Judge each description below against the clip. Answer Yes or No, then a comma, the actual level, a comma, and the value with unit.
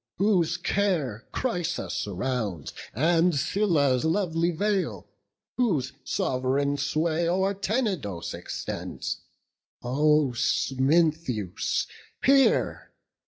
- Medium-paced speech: No, slow, 75 wpm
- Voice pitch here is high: No, medium, 160 Hz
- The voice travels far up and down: Yes, wide, 6.2 semitones